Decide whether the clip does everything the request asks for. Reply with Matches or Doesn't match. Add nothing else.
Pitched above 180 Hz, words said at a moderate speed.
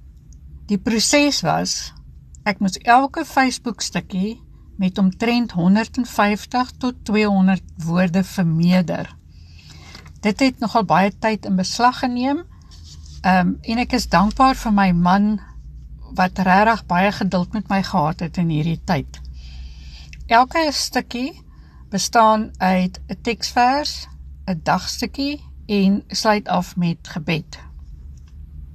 Doesn't match